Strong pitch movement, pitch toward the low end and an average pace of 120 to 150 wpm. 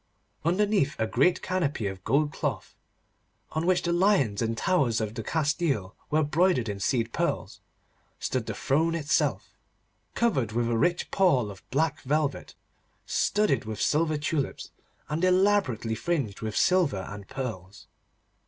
No: wide, 7.3 semitones; medium, 145 Hz; average, 140 wpm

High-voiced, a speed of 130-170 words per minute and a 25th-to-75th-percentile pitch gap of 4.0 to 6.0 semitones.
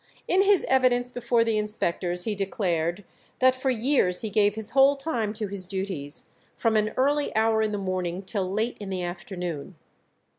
No: high, 210 Hz; average, 180 wpm; average, 4.8 semitones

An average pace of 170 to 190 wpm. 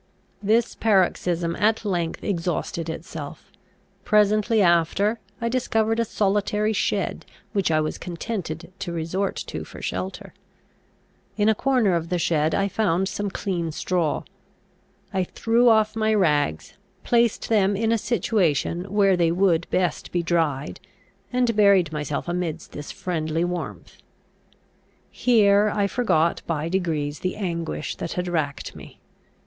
No: slow, 135 wpm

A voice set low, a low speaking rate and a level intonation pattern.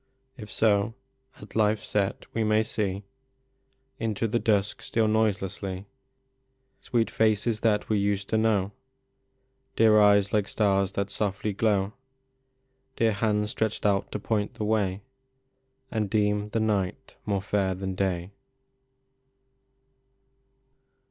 Yes: low, 105 Hz; slow, 125 wpm; narrow, 1.8 semitones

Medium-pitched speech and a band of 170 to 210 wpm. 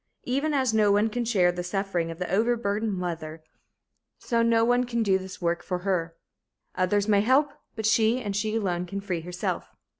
No: high, 205 Hz; average, 190 wpm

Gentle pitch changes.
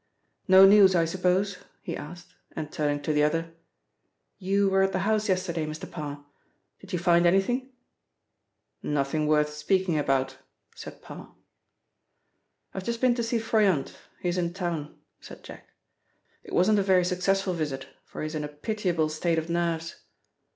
No: average, 3.9 semitones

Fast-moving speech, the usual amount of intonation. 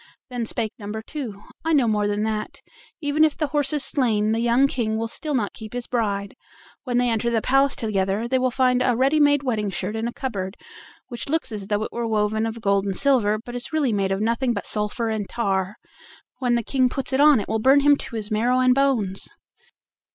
Yes: fast, 230 wpm; average, 3.8 semitones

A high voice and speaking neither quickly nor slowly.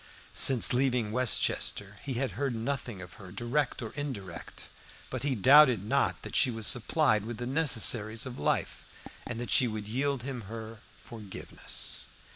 No: low, 120 Hz; average, 160 wpm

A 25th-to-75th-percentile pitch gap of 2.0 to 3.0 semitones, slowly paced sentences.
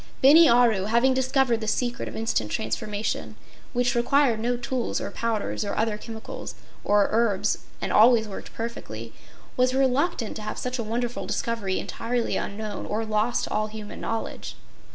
No: narrow, 2.5 semitones; average, 160 wpm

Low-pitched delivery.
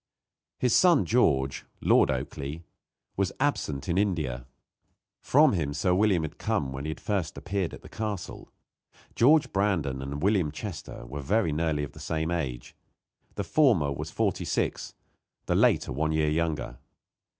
Yes: very low, 80 Hz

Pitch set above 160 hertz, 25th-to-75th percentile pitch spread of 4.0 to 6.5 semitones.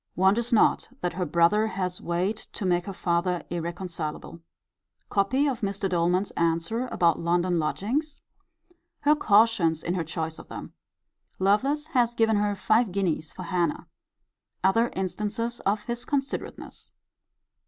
Yes: high, 190 Hz; average, 4.7 semitones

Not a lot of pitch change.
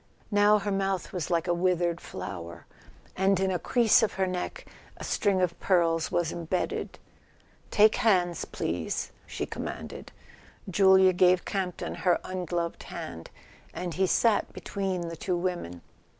Yes: narrow, 2.2 semitones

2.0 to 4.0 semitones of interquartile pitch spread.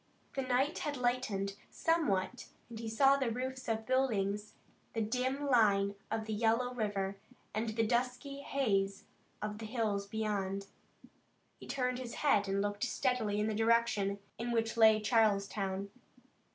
Yes: average, 3.6 semitones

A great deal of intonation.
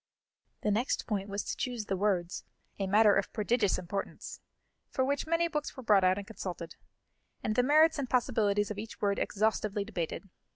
No: average, 3.8 semitones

